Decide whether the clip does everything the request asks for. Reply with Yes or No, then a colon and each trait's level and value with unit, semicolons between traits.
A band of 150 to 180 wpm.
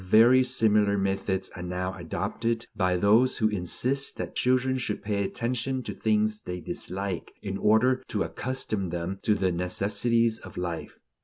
Yes: average, 155 wpm